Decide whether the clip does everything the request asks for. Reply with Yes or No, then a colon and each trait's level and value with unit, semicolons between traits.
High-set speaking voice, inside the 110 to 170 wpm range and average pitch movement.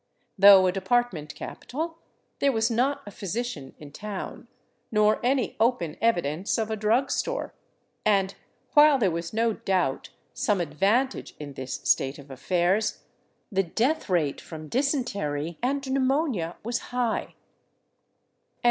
No: high, 210 Hz; average, 140 wpm; wide, 6.3 semitones